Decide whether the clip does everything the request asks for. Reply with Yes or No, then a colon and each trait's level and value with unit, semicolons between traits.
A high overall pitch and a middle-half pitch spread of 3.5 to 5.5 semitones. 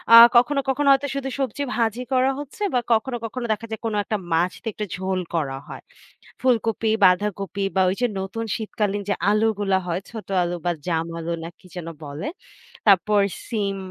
Yes: high, 210 Hz; average, 4.3 semitones